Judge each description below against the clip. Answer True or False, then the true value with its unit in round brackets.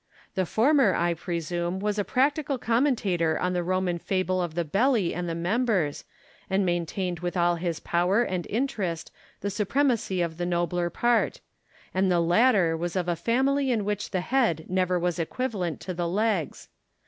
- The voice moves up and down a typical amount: True (4.2 semitones)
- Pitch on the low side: False (185 Hz)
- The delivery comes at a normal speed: True (170 wpm)